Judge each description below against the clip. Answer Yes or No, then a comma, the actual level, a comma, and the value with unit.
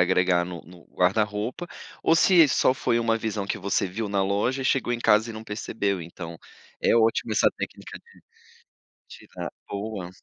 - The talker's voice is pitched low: Yes, low, 105 Hz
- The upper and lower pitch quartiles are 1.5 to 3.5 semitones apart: No, average, 3.9 semitones